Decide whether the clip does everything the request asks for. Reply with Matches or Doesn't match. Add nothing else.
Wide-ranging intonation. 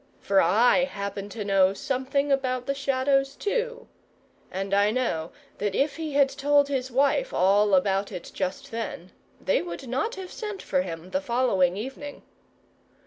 Matches